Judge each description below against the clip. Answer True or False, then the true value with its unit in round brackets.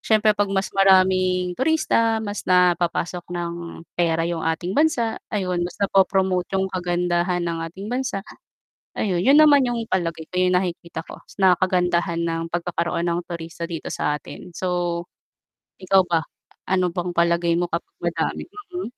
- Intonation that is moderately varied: False (2.2 semitones)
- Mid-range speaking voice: True (180 Hz)